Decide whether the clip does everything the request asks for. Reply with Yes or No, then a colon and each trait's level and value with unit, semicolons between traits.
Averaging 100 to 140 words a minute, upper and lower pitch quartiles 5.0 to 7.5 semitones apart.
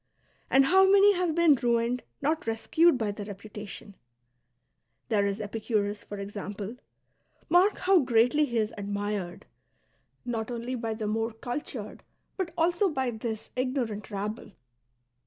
Yes: slow, 135 wpm; wide, 5.5 semitones